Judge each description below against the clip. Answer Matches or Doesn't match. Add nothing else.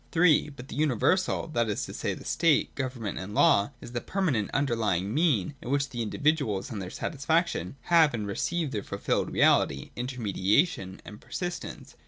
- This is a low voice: Matches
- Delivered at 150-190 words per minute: Matches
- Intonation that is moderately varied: Doesn't match